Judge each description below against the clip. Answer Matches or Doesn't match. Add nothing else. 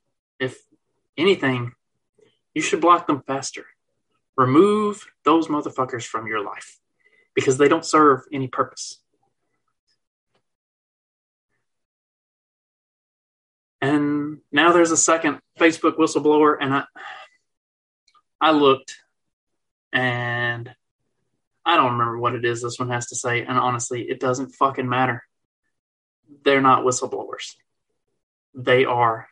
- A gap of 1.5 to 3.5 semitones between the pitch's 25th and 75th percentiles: Doesn't match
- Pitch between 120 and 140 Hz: Matches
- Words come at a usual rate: Doesn't match